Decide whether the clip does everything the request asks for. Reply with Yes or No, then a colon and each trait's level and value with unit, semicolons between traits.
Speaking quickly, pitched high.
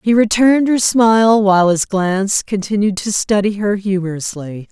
No: average, 155 wpm; high, 205 Hz